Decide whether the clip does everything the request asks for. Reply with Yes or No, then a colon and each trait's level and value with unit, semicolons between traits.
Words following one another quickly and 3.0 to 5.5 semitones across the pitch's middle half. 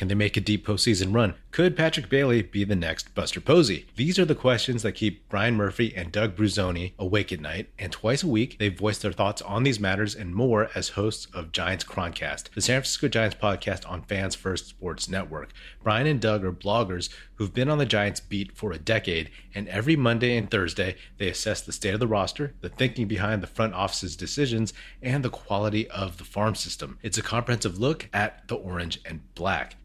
Yes: fast, 215 wpm; average, 3.6 semitones